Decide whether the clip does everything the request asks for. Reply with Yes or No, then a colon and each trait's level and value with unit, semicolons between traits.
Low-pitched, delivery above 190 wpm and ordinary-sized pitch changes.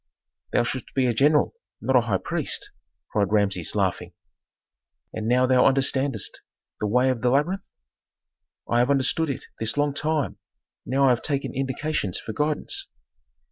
No: low, 130 Hz; average, 155 wpm; average, 3.5 semitones